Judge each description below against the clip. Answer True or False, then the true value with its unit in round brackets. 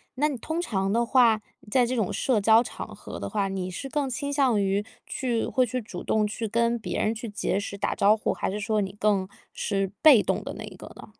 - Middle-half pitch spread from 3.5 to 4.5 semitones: True (3.9 semitones)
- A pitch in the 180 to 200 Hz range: False (220 Hz)